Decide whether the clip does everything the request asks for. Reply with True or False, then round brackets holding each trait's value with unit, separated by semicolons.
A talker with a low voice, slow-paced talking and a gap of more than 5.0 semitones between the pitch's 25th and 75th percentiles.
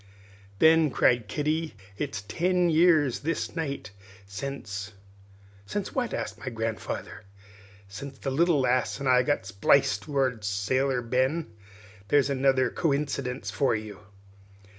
True (130 Hz; 125 wpm; 5.5 semitones)